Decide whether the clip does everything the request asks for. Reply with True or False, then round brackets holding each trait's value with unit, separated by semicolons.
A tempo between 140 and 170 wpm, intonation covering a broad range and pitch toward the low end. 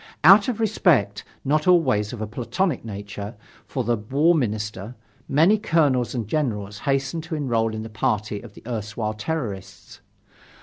True (150 wpm; 6.4 semitones; 120 Hz)